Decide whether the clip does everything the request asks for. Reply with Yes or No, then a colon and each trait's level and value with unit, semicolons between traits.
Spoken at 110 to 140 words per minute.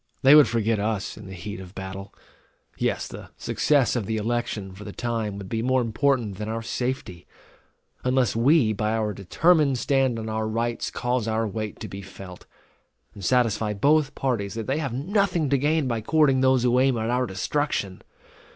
No: average, 190 wpm